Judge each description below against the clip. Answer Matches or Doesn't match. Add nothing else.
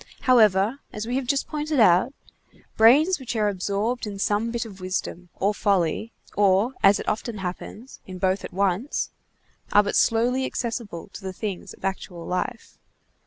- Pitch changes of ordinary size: Matches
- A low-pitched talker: Doesn't match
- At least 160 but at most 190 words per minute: Matches